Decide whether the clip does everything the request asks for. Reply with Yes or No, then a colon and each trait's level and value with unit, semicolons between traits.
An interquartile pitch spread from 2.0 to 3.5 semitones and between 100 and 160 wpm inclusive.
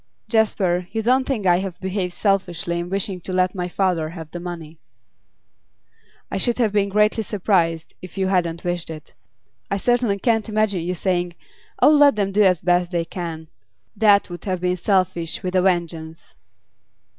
No: average, 2.7 semitones; average, 180 wpm